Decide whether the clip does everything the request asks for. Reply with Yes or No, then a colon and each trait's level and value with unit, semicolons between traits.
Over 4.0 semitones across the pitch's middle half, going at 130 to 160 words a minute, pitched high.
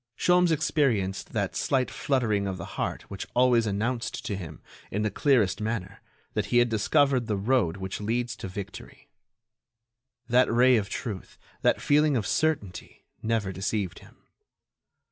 No: average, 4.4 semitones; average, 150 wpm; low, 115 Hz